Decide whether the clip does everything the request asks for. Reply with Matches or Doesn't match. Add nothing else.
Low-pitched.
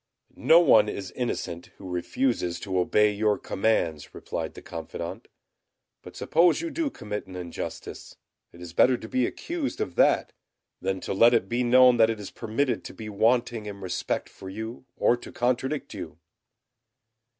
Matches